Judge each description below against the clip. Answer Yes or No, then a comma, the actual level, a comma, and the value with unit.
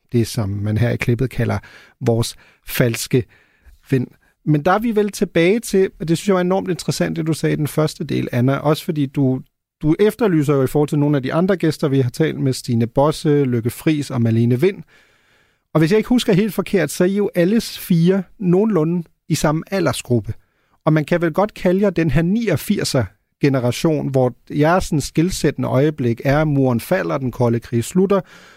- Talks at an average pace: Yes, average, 205 wpm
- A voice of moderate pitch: Yes, medium, 155 Hz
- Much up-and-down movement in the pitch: Yes, wide, 5.9 semitones